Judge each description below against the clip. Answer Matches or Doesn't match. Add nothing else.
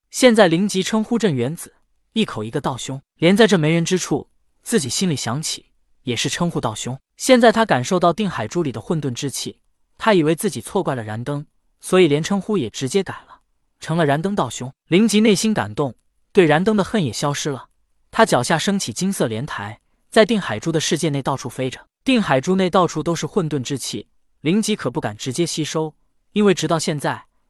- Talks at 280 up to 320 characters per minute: Matches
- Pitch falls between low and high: Matches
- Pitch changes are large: Matches